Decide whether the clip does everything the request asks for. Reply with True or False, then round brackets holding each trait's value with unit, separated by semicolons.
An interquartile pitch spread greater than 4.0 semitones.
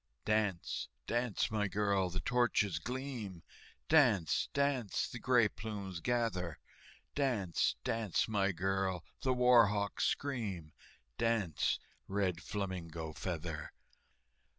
True (4.7 semitones)